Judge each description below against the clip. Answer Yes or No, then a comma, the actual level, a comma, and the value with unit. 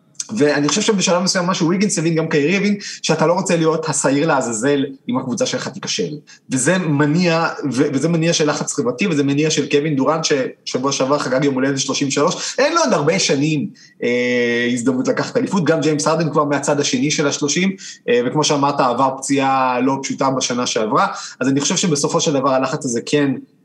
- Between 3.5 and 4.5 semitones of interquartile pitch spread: No, average, 3.1 semitones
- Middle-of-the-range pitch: Yes, medium, 150 Hz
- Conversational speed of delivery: No, fast, 190 wpm